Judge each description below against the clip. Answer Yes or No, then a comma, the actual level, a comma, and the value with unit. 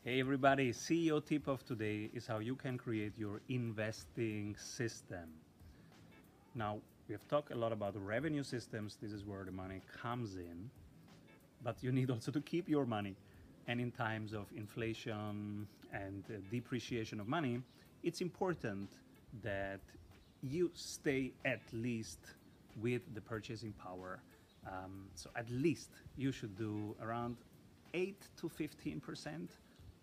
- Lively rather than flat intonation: No, average, 4.0 semitones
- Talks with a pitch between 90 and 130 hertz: Yes, low, 115 Hz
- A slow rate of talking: No, average, 145 wpm